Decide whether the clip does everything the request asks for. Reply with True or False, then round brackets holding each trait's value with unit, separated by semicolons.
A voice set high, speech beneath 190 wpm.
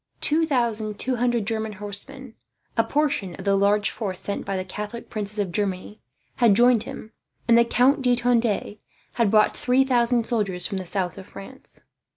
True (220 Hz; 180 wpm)